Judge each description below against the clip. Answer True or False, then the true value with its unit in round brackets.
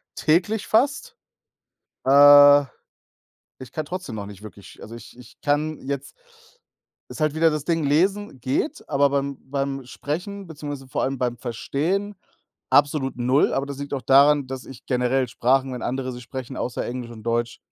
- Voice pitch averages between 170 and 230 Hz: False (140 Hz)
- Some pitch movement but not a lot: True (3.4 semitones)